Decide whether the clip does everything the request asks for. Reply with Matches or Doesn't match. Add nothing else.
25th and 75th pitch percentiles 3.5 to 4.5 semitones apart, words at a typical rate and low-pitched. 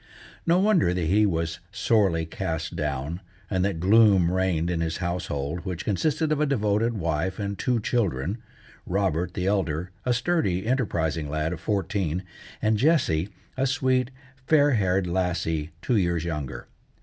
Doesn't match